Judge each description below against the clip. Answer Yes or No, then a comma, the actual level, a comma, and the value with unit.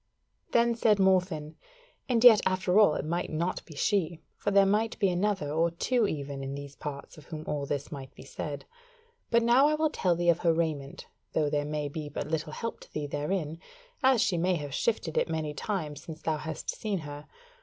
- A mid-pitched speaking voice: Yes, medium, 165 Hz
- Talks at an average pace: No, fast, 210 wpm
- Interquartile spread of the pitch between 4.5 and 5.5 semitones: Yes, average, 5.1 semitones